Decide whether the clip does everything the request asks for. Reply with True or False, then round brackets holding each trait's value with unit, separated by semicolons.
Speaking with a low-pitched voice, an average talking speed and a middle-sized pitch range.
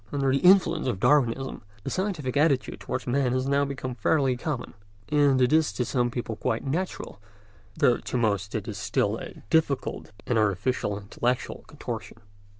True (130 Hz; 160 wpm; 3.7 semitones)